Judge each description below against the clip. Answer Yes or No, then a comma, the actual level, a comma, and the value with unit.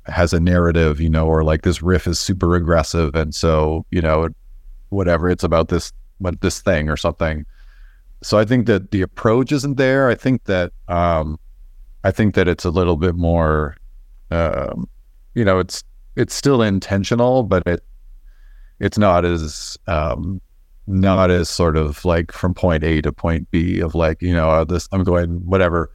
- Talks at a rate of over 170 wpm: Yes, average, 180 wpm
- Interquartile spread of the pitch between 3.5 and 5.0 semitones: No, average, 3.0 semitones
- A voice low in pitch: Yes, very low, 85 Hz